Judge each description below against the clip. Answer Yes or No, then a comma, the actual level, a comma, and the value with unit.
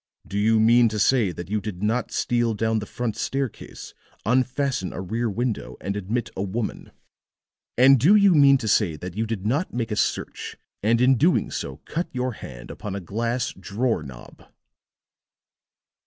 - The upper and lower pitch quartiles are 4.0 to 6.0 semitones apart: No, average, 3.6 semitones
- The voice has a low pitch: Yes, low, 115 Hz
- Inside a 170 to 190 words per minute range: Yes, average, 175 wpm